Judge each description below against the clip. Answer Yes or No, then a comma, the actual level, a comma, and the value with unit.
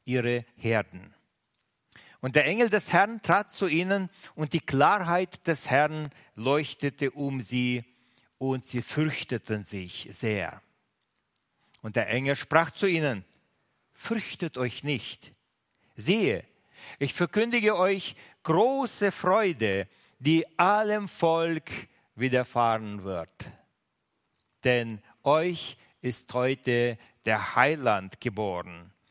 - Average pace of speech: No, slow, 105 wpm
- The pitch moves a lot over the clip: Yes, wide, 5.9 semitones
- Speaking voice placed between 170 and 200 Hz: No, low, 135 Hz